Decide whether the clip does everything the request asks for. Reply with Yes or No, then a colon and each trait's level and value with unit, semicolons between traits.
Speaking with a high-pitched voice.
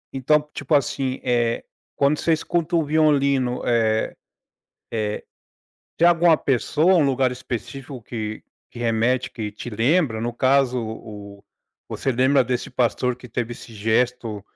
No: low, 125 Hz